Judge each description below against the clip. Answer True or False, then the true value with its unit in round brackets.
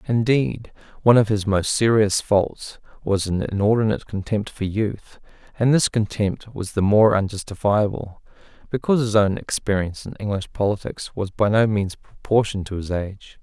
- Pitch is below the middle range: True (105 Hz)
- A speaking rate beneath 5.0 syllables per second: False (5.1 syllables/s)